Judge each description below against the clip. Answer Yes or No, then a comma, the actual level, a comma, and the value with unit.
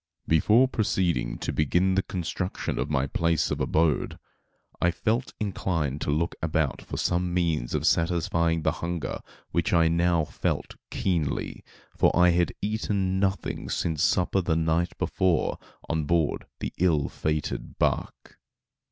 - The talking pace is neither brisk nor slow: Yes, average, 145 wpm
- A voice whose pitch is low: Yes, very low, 85 Hz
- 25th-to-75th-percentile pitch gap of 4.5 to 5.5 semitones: No, narrow, 2.5 semitones